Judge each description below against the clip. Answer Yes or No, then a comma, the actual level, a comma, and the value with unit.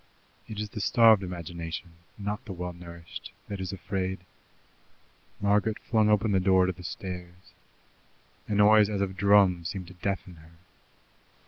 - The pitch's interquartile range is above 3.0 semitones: No, narrow, 2.5 semitones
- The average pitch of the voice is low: Yes, very low, 95 Hz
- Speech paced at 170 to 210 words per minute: No, average, 150 wpm